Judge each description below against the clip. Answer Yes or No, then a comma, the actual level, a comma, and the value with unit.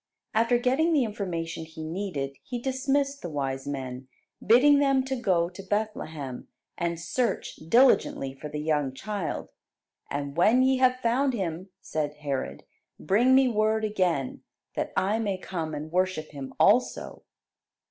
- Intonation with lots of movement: Yes, wide, 8.0 semitones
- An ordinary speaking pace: Yes, average, 145 wpm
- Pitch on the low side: No, high, 190 Hz